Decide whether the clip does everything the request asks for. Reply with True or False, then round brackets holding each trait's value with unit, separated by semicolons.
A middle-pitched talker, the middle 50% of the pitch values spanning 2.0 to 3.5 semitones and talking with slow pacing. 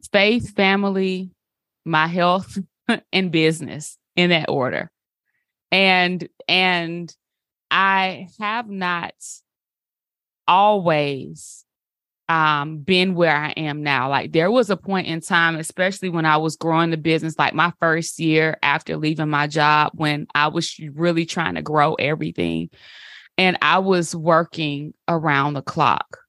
True (165 Hz; 3.2 semitones; 130 wpm)